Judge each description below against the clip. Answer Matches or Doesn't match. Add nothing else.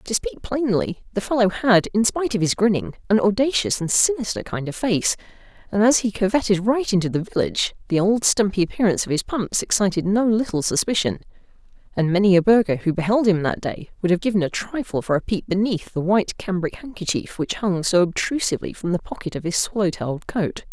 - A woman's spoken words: Matches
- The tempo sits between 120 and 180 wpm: Doesn't match